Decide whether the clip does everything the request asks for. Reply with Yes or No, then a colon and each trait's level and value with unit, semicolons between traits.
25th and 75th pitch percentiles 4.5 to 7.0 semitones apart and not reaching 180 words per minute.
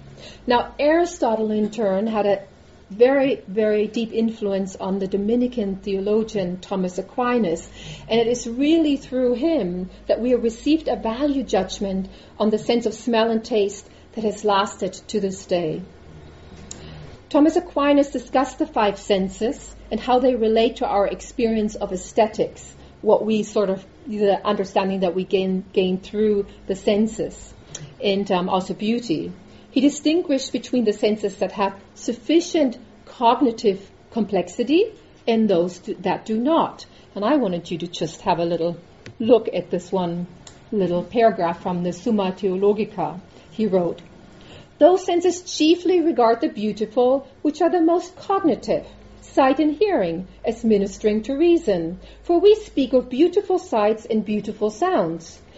Yes: average, 5.2 semitones; average, 150 wpm